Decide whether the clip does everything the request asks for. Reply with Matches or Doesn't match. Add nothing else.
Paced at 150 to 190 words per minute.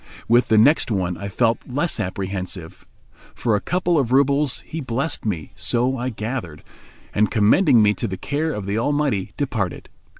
Matches